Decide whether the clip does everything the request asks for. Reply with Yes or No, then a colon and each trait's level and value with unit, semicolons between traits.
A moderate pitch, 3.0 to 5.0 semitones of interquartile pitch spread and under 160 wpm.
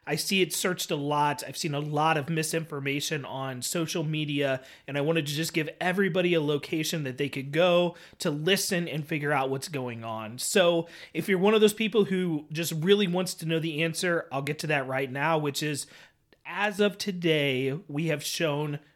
No: medium, 160 Hz; average, 3.3 semitones; fast, 205 wpm